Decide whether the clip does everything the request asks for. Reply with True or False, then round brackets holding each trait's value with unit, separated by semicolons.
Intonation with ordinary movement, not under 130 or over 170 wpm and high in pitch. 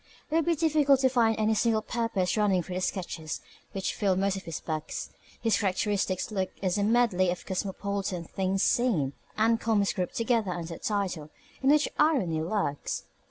False (4.0 semitones; 180 wpm; 200 Hz)